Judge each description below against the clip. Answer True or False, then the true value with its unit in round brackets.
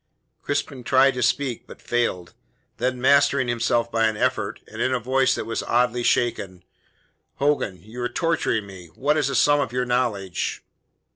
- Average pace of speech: True (185 wpm)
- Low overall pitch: True (120 Hz)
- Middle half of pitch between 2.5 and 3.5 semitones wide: True (2.9 semitones)